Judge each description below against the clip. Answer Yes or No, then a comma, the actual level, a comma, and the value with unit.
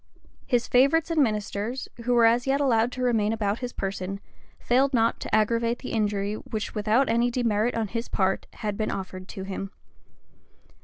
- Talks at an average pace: Yes, average, 175 wpm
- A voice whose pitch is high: Yes, high, 225 Hz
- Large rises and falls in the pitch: No, average, 3.0 semitones